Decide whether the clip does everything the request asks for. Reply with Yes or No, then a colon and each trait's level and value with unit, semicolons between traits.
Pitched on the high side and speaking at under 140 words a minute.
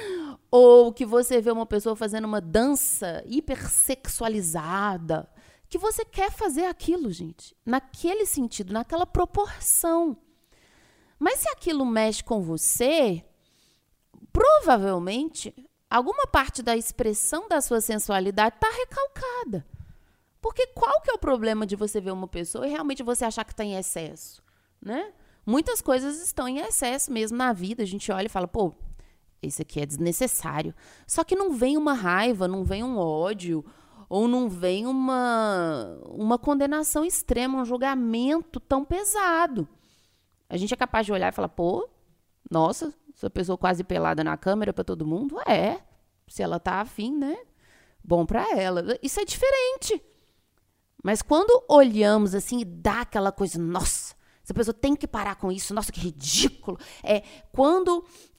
No: high, 240 Hz; average, 150 wpm